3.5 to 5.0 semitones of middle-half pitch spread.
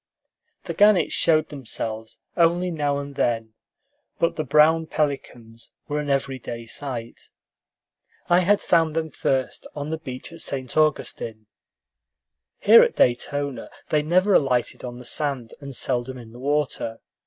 Yes: average, 4.3 semitones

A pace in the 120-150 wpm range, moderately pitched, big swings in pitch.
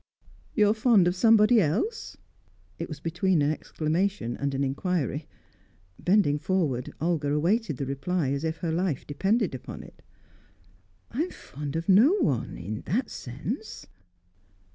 Yes: average, 145 wpm; medium, 165 Hz; wide, 6.3 semitones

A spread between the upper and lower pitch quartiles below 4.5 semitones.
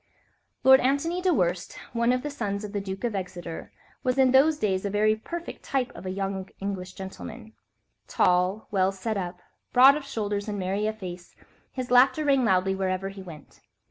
No: average, 5.1 semitones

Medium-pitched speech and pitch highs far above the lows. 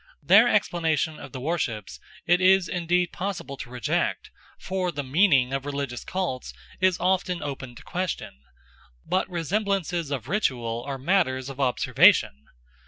Yes: medium, 155 Hz; wide, 5.8 semitones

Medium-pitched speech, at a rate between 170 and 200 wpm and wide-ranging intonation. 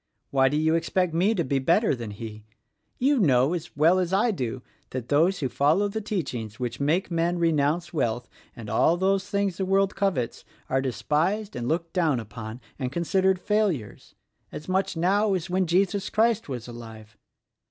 Yes: medium, 165 Hz; average, 185 wpm; wide, 6.8 semitones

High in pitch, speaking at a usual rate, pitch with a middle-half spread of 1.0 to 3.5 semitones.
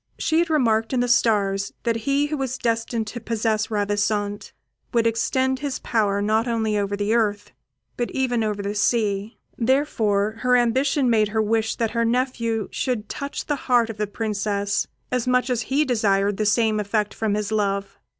Yes: high, 225 Hz; average, 180 wpm; average, 3.1 semitones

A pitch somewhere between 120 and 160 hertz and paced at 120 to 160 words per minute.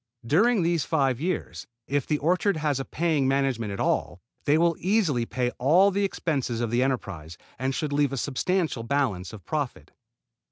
No: medium, 140 Hz; average, 175 wpm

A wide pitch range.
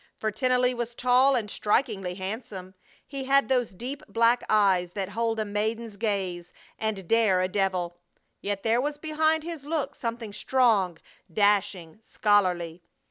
No: average, 4.5 semitones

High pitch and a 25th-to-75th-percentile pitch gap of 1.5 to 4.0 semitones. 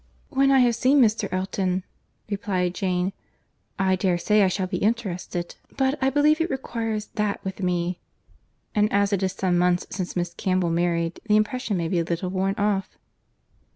Yes: high, 195 Hz; average, 3.3 semitones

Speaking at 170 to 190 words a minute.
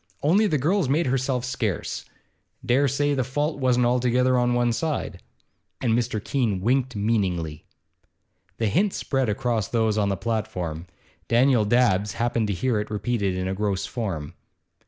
No: average, 155 wpm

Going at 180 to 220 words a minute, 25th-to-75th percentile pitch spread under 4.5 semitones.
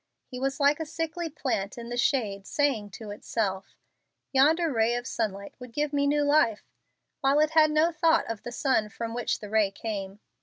No: average, 195 wpm; wide, 5.5 semitones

